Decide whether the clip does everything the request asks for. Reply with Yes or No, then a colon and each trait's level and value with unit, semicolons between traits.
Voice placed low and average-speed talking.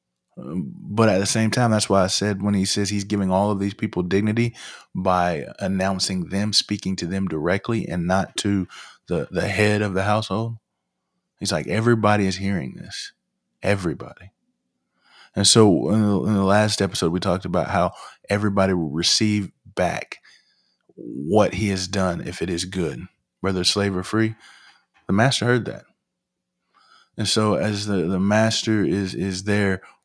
Yes: low, 100 Hz; average, 165 wpm